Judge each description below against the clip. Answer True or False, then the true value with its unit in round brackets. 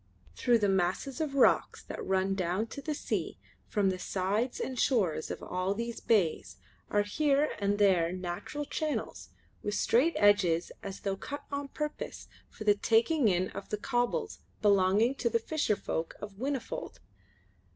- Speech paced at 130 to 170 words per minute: True (160 wpm)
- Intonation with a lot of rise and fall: True (5.7 semitones)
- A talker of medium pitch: False (210 Hz)